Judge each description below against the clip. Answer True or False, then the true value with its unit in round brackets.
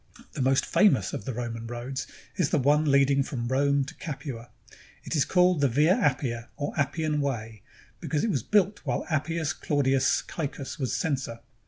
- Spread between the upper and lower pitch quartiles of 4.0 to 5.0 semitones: False (3.2 semitones)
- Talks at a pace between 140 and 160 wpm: False (180 wpm)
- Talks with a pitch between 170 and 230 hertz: False (140 Hz)